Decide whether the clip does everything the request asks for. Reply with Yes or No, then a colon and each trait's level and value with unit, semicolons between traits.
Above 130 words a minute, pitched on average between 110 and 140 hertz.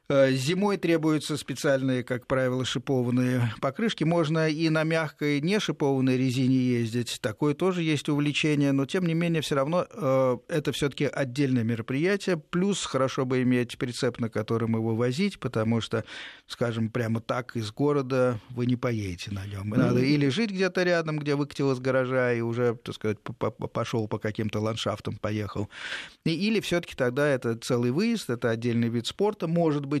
Yes: fast, 160 wpm; low, 135 Hz